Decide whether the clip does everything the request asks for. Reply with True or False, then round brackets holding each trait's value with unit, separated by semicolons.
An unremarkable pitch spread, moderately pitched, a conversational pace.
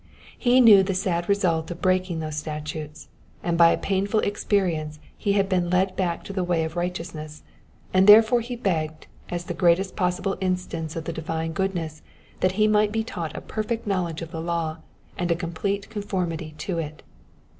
True (3.3 semitones; 180 Hz; 185 wpm)